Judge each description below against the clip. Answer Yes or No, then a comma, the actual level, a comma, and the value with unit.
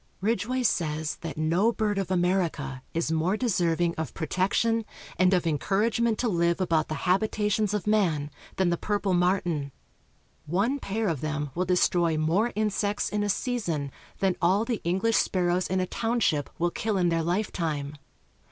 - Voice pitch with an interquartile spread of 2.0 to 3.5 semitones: No, average, 4.2 semitones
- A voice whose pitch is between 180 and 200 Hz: Yes, medium, 185 Hz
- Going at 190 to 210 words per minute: No, average, 165 wpm